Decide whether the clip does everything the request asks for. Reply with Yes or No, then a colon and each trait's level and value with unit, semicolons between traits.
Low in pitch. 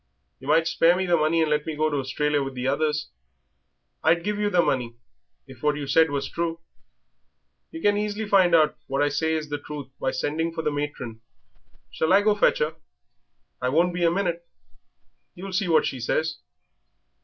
No: medium, 160 Hz